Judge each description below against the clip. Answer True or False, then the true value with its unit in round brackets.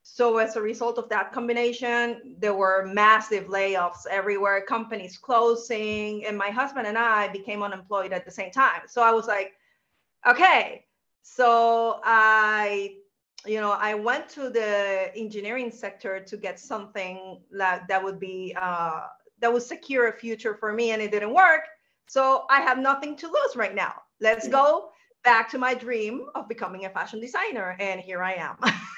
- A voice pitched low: False (220 Hz)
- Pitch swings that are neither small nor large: True (3.4 semitones)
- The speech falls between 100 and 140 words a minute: False (170 wpm)